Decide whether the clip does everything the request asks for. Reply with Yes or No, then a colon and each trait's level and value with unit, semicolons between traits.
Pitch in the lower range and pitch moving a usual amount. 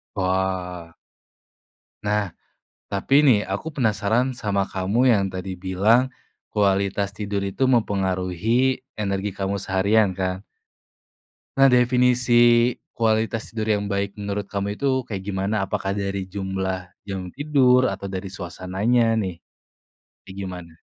Yes: low, 100 Hz; average, 3.4 semitones